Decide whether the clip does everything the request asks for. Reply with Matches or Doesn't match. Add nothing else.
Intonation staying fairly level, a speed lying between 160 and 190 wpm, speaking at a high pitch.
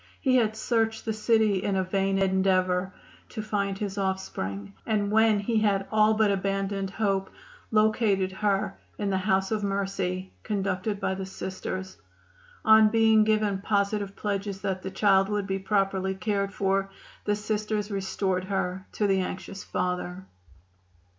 Doesn't match